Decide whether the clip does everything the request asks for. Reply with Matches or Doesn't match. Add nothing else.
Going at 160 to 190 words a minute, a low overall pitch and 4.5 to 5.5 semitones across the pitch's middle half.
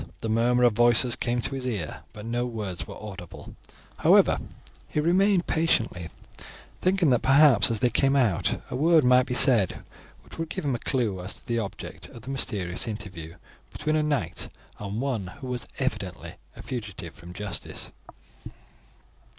Matches